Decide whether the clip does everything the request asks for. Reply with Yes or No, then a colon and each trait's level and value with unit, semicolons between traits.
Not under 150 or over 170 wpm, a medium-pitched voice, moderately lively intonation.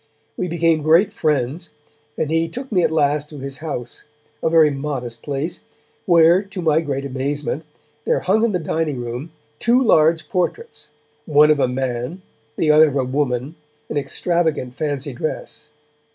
Yes: average, 165 wpm; medium, 150 Hz; average, 3.3 semitones